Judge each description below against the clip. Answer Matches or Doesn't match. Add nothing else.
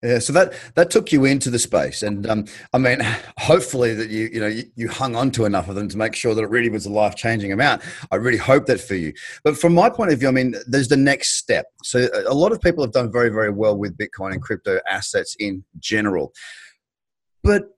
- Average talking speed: Doesn't match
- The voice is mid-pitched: Doesn't match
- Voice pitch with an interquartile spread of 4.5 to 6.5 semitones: Matches